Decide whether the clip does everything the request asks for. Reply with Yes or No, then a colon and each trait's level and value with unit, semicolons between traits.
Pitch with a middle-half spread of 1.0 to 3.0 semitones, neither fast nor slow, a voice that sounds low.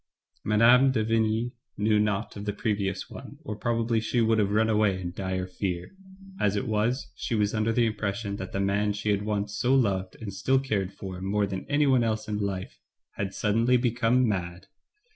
Yes: average, 2.7 semitones; average, 195 wpm; low, 105 Hz